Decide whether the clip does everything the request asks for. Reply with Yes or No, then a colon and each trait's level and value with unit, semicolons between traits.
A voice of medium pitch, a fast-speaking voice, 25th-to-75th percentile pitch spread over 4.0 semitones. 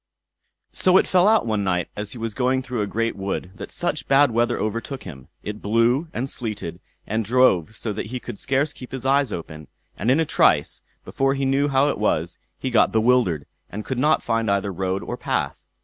No: low, 115 Hz; fast, 210 wpm; average, 4.8 semitones